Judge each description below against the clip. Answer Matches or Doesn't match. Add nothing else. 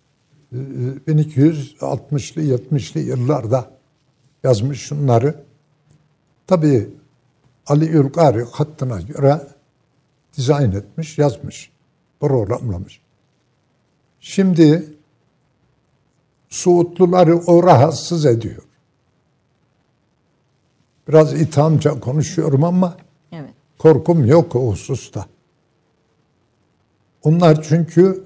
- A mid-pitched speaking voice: Matches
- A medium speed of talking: Doesn't match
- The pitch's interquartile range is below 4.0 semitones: Matches